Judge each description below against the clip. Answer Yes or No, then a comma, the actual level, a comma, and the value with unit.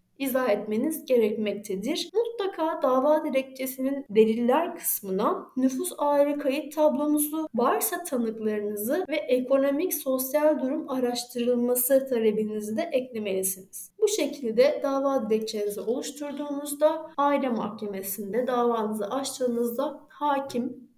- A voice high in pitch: Yes, very high, 260 Hz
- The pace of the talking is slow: Yes, slow, 90 wpm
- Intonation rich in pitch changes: No, average, 4.6 semitones